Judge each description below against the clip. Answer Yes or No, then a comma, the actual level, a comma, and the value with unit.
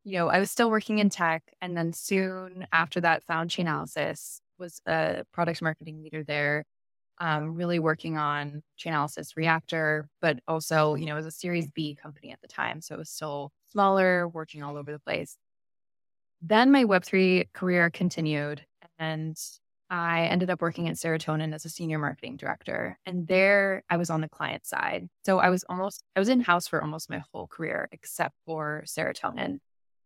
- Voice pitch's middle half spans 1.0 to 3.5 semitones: Yes, average, 2.8 semitones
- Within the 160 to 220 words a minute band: Yes, average, 180 wpm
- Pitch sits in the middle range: Yes, medium, 165 Hz